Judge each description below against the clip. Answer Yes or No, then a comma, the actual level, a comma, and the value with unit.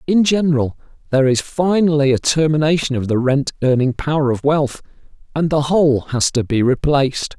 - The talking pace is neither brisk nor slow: Yes, average, 170 wpm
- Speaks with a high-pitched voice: No, medium, 145 Hz